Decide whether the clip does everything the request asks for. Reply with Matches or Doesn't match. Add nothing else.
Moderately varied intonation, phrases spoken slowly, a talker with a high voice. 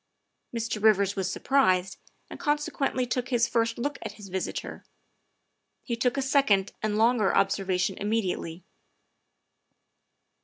Matches